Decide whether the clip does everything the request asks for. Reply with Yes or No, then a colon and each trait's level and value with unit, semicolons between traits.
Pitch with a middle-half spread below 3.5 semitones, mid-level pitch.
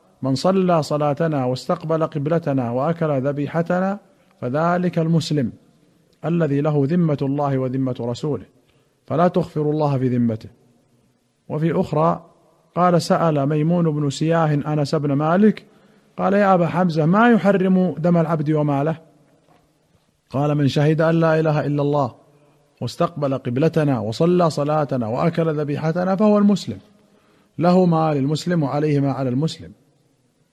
Yes: average, 3.0 semitones; medium, 155 Hz